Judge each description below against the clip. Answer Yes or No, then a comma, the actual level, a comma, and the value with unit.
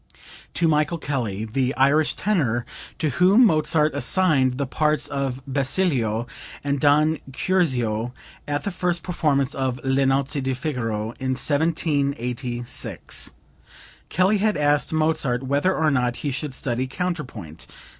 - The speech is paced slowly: Yes, slow, 130 wpm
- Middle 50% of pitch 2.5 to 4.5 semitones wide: Yes, average, 3.7 semitones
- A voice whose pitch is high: No, medium, 140 Hz